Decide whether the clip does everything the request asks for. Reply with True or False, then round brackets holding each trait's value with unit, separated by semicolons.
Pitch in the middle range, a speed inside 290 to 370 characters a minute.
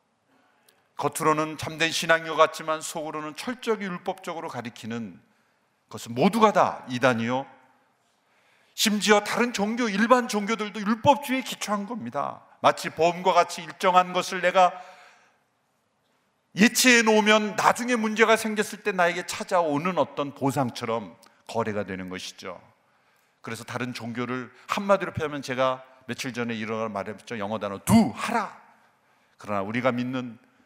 True (165 Hz; 305 characters per minute)